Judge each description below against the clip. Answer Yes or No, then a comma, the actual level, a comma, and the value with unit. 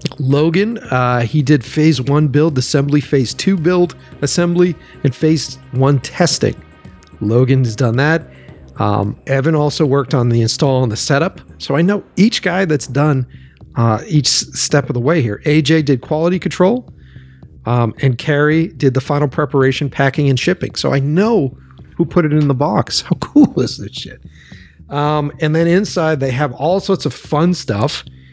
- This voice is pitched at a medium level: Yes, medium, 145 Hz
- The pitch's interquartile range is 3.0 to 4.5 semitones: Yes, average, 4.1 semitones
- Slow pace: No, average, 175 wpm